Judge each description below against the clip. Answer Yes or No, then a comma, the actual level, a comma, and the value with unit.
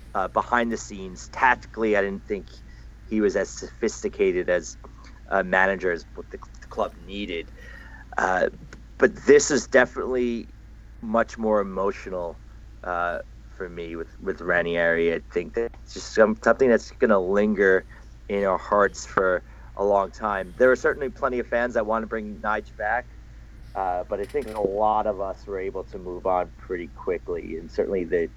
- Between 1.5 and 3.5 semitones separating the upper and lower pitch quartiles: No, average, 4.4 semitones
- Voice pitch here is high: No, low, 105 Hz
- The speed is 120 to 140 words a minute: No, average, 175 wpm